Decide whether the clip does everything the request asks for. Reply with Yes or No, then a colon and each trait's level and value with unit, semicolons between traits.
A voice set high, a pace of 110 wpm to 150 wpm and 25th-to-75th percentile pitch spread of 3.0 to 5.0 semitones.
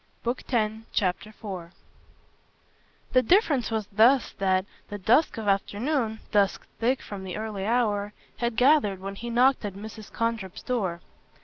Yes: high, 220 Hz; average, 145 wpm; average, 3.4 semitones